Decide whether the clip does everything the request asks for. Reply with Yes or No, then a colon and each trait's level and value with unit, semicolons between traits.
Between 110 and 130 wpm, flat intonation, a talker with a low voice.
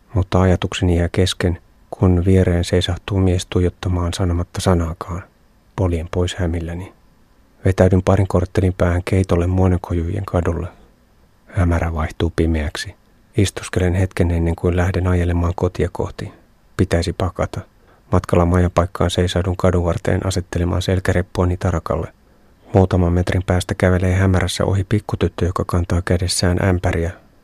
Yes: average, 115 wpm; narrow, 1.6 semitones; very low, 90 Hz